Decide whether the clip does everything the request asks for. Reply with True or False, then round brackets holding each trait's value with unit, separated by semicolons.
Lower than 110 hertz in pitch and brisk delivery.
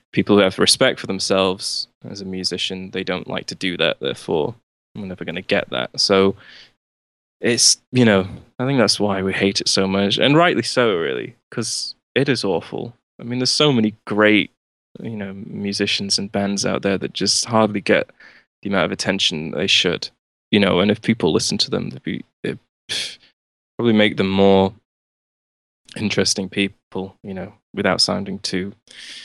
False (100 Hz; 180 wpm)